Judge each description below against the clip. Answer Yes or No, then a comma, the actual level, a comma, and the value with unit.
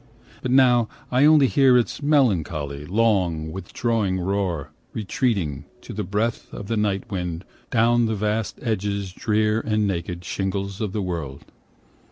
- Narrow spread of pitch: No, average, 4.1 semitones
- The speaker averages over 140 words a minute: Yes, average, 150 wpm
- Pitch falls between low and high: No, low, 100 Hz